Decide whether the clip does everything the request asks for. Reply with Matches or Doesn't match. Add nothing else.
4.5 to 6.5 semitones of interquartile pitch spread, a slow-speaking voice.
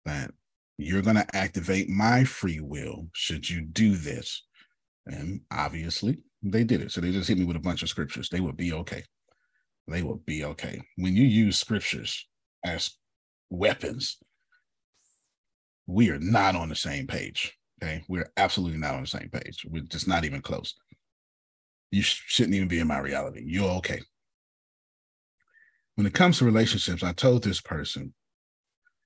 Doesn't match